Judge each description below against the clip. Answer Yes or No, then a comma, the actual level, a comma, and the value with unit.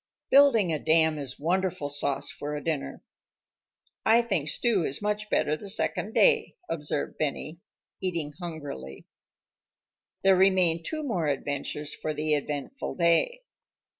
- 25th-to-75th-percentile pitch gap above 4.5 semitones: Yes, average, 4.9 semitones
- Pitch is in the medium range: Yes, medium, 165 Hz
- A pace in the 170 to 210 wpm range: No, slow, 135 wpm